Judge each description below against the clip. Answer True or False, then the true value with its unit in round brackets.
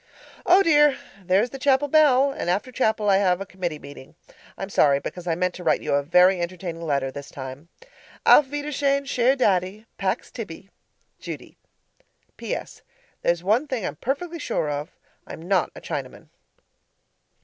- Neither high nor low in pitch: False (195 Hz)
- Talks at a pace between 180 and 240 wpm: False (160 wpm)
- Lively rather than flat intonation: True (7.8 semitones)